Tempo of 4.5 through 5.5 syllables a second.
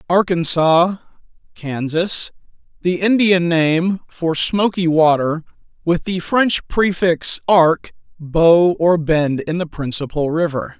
No: 3.5 syllables/s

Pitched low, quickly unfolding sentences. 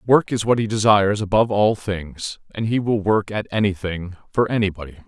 No: low, 105 Hz; average, 190 wpm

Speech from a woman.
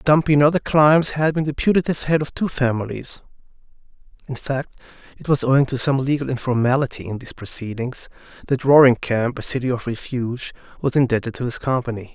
No: male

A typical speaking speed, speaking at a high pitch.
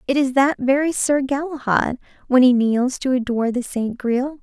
Yes: average, 190 wpm; very high, 260 Hz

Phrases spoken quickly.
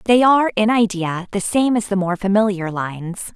No: average, 195 wpm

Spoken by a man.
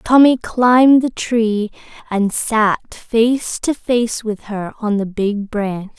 No: female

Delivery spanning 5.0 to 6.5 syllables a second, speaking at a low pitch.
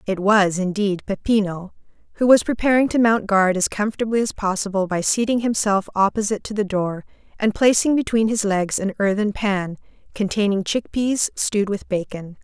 No: 5.3 syllables/s; high, 205 Hz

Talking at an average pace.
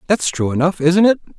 No: fast, 215 wpm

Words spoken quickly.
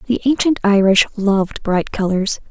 No: average, 145 wpm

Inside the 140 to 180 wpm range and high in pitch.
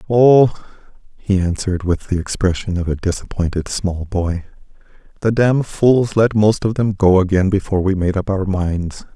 No: average, 170 wpm; low, 100 Hz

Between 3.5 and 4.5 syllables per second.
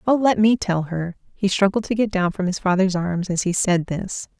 No: 5.0 syllables/s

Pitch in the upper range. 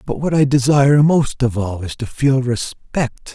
No: low, 130 Hz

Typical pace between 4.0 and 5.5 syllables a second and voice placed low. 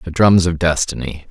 Yes: 5.1 syllables/s; very low, 85 Hz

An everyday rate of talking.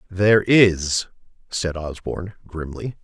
No: slow, 100 wpm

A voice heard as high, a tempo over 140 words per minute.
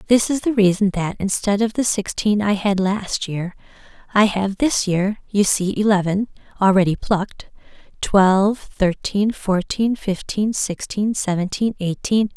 No: high, 200 Hz; slow, 135 wpm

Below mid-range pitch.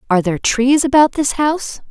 No: very high, 260 Hz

